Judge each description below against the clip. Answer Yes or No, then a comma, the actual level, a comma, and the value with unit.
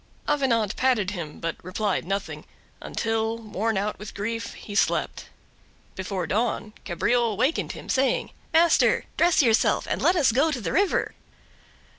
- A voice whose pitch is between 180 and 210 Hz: No, high, 225 Hz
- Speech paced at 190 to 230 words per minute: No, average, 145 wpm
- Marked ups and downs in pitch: No, average, 4.4 semitones